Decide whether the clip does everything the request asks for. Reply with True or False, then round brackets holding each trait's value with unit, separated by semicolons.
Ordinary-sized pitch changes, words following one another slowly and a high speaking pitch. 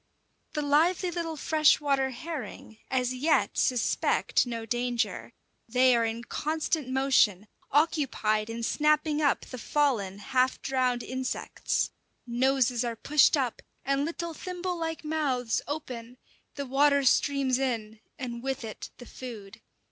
True (3.9 semitones; 130 wpm; 260 Hz)